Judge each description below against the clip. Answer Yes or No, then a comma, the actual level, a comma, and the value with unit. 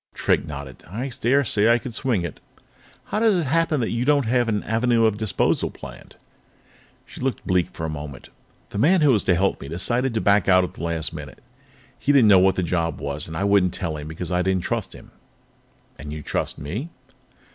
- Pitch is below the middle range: Yes, low, 100 Hz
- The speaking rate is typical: No, fast, 220 wpm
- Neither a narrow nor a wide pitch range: No, wide, 6.8 semitones